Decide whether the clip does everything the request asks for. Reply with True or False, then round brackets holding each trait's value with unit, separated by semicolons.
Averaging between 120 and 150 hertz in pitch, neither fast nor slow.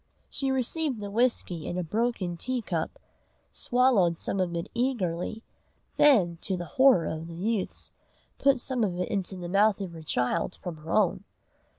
False (195 Hz; 175 wpm)